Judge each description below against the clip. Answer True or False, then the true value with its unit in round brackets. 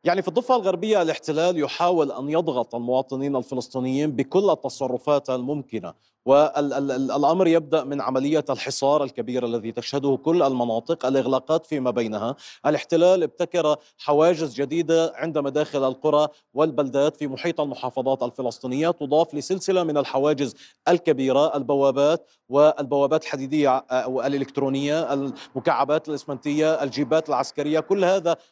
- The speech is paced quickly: False (115 wpm)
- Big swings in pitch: False (3.1 semitones)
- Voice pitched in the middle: True (145 Hz)